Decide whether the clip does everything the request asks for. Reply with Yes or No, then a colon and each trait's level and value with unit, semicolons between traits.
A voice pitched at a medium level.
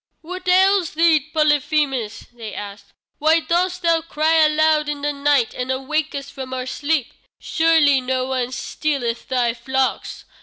No: very high, 290 Hz